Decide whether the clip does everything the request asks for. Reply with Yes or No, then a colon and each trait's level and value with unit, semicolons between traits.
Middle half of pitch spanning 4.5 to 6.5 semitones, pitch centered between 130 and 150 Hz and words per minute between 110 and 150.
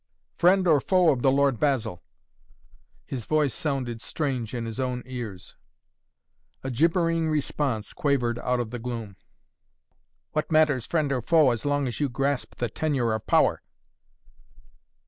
No: average, 4.0 semitones; low, 135 Hz; average, 145 wpm